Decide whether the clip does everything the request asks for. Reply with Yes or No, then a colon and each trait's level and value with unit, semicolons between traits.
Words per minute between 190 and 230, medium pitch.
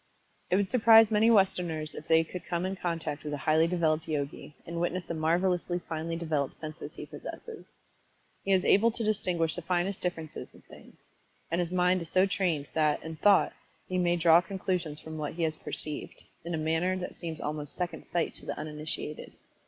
Yes: average, 195 wpm; medium, 170 Hz